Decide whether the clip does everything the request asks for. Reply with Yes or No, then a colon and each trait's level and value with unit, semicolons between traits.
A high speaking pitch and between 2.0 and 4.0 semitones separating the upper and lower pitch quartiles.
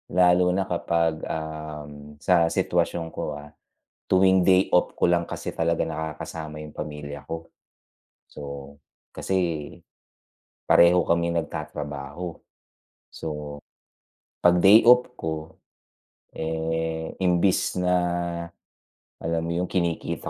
No: very low, 80 Hz; narrow, 2.6 semitones